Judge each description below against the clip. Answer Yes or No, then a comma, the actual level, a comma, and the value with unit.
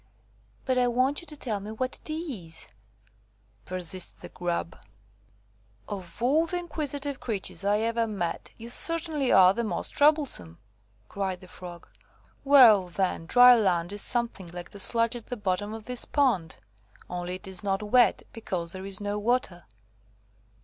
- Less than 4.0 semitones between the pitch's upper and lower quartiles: No, wide, 5.5 semitones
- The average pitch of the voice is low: No, high, 210 Hz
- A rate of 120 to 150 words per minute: No, average, 160 wpm